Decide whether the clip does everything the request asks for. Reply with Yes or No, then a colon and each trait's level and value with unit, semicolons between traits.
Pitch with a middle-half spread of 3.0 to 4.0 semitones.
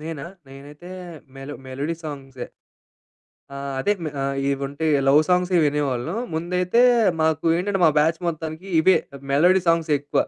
Yes: average, 3.7 semitones